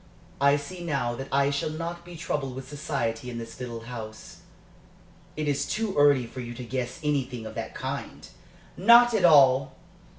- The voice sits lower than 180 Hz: Yes, medium, 140 Hz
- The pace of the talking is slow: No, average, 175 wpm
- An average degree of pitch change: Yes, average, 3.8 semitones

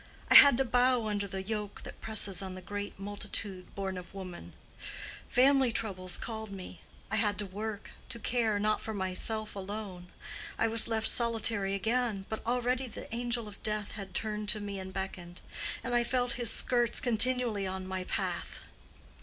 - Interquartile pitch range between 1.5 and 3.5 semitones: Yes, average, 3.2 semitones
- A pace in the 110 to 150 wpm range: No, average, 170 wpm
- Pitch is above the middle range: Yes, high, 210 Hz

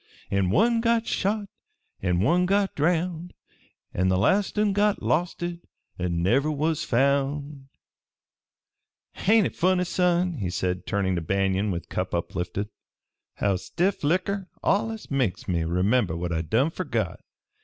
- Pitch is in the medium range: Yes, medium, 145 Hz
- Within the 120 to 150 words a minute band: Yes, average, 140 wpm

